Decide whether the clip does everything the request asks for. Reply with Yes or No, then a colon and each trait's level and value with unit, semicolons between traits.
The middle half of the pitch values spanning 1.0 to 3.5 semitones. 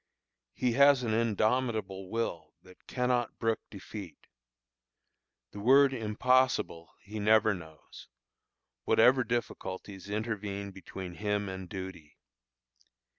No: average, 3.9 semitones